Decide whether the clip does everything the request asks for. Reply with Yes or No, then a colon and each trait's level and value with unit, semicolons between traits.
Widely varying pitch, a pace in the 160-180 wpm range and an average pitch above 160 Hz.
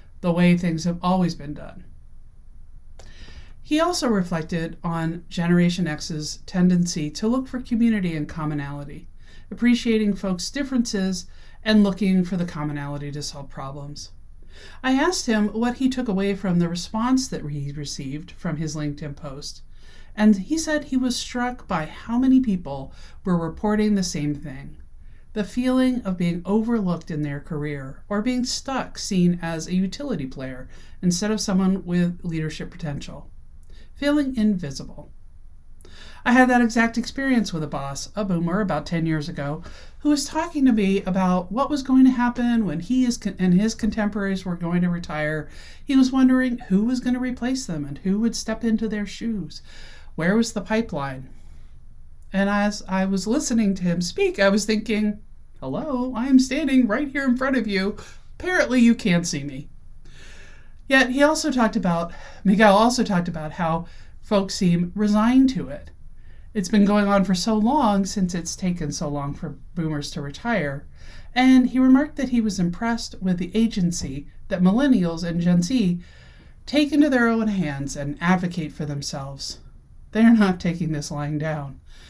Yes: wide, 7.0 semitones; average, 170 wpm; high, 190 Hz